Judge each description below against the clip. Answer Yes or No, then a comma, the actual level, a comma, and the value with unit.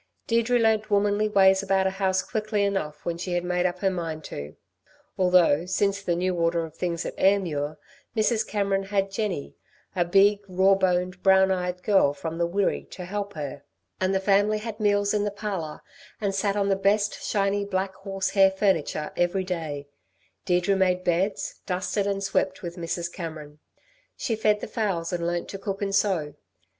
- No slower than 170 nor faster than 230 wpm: Yes, average, 185 wpm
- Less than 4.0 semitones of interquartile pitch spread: Yes, narrow, 2.5 semitones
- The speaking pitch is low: No, high, 190 Hz